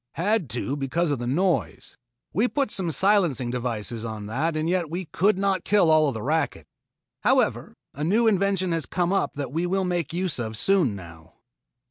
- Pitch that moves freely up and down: Yes, wide, 6.9 semitones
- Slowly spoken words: No, average, 190 wpm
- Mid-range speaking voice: Yes, medium, 165 Hz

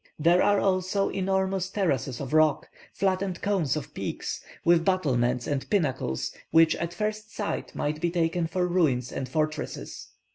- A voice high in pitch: No, medium, 170 Hz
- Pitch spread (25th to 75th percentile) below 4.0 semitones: No, average, 4.4 semitones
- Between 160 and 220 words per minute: No, average, 150 wpm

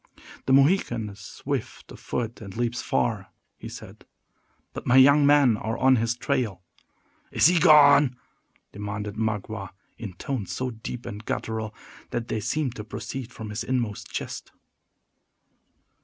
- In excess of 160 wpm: No, average, 145 wpm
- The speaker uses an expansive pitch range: No, average, 3.8 semitones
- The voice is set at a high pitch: No, low, 115 Hz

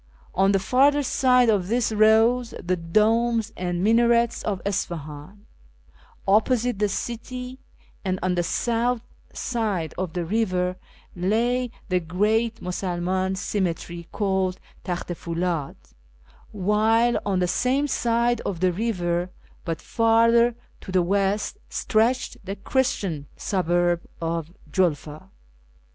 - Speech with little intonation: No, average, 4.5 semitones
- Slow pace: Yes, slow, 125 wpm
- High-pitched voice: Yes, high, 200 Hz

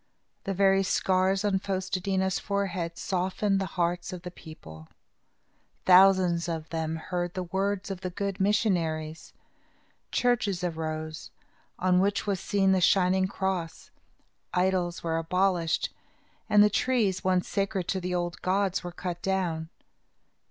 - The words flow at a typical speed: Yes, average, 145 wpm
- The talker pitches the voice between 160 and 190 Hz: Yes, medium, 185 Hz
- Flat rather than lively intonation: Yes, narrow, 2.0 semitones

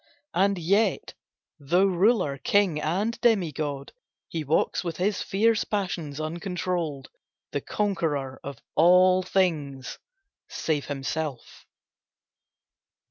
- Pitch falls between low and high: Yes, medium, 175 Hz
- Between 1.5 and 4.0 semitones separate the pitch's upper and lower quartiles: No, average, 5.1 semitones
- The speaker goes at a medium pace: No, slow, 95 wpm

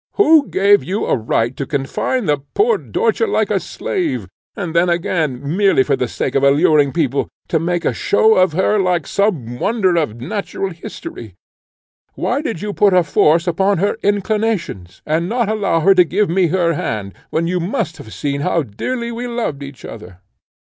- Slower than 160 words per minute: No, average, 185 wpm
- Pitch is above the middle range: No, medium, 175 Hz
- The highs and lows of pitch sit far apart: Yes, wide, 6.3 semitones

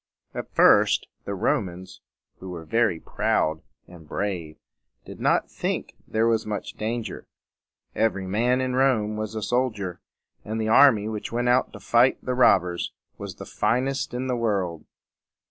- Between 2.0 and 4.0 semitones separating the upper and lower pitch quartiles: No, average, 4.5 semitones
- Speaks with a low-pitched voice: Yes, low, 110 Hz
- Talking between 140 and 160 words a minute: Yes, average, 155 wpm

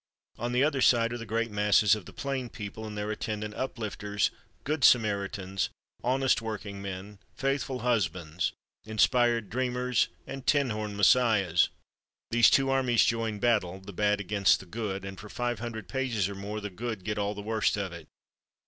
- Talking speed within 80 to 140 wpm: No, average, 170 wpm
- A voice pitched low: Yes, low, 110 Hz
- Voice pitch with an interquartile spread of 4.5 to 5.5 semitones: No, average, 3.2 semitones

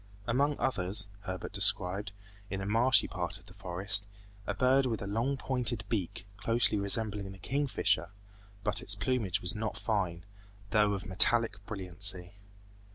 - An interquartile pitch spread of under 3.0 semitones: No, average, 3.3 semitones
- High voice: No, low, 105 Hz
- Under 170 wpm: Yes, average, 160 wpm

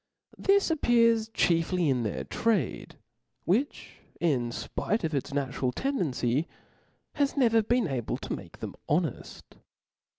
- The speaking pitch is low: No, medium, 175 Hz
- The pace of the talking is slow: Yes, slow, 125 wpm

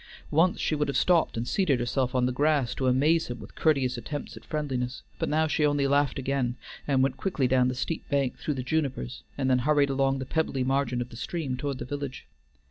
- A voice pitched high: No, low, 135 Hz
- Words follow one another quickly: Yes, fast, 225 wpm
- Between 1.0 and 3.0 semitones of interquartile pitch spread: Yes, narrow, 2.6 semitones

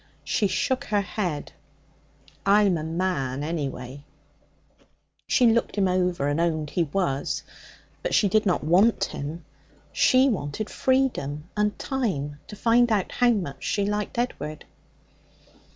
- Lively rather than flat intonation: Yes, wide, 6.3 semitones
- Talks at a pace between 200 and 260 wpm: No, slow, 135 wpm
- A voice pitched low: No, medium, 185 Hz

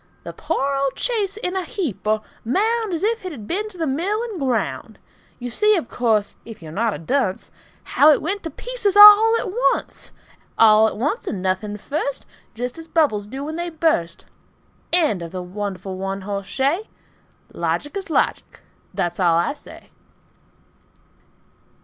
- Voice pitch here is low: No, very high, 280 Hz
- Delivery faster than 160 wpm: Yes, average, 175 wpm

